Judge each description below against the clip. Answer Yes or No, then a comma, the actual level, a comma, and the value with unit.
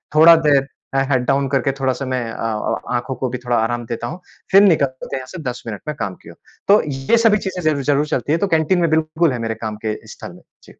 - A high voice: No, low, 135 Hz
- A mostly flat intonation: No, average, 4.7 semitones